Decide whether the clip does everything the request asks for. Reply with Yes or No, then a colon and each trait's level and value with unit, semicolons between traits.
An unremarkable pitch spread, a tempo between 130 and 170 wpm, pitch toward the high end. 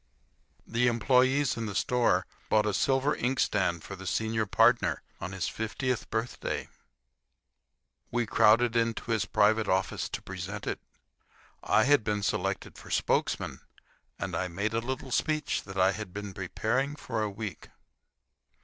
No: average, 3.6 semitones; average, 150 wpm; low, 110 Hz